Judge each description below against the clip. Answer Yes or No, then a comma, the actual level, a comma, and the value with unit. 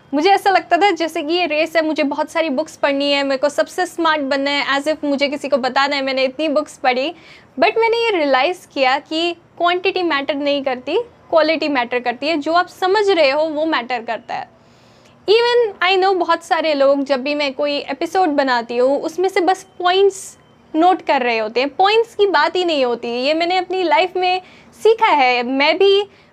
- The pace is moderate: No, fast, 210 wpm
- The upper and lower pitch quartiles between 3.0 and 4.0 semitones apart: No, average, 4.5 semitones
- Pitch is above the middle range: Yes, very high, 315 Hz